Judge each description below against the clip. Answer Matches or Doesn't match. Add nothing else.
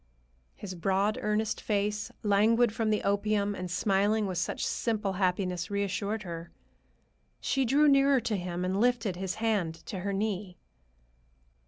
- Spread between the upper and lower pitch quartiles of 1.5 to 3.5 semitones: Matches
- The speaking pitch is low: Doesn't match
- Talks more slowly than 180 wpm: Matches